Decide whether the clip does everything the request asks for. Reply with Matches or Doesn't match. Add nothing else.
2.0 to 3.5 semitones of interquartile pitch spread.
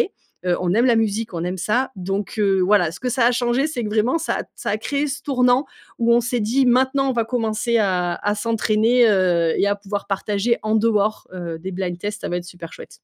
Doesn't match